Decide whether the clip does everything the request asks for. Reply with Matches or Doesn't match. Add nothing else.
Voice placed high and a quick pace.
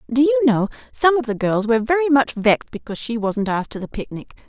Matches